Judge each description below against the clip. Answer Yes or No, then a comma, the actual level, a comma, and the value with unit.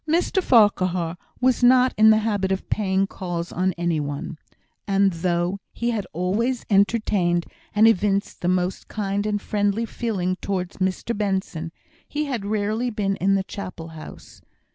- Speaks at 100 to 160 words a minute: Yes, average, 155 wpm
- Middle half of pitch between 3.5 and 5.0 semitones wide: No, average, 3.1 semitones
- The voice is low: No, high, 195 Hz